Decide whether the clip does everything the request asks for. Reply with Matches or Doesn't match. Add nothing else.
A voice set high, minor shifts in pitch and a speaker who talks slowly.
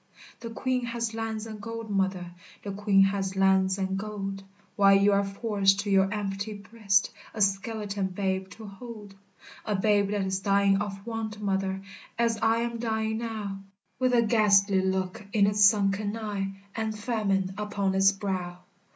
Doesn't match